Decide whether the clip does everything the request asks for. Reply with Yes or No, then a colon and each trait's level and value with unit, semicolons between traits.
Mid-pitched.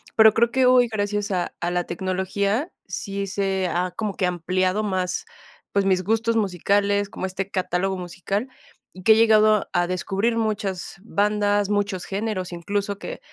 No: high, 200 Hz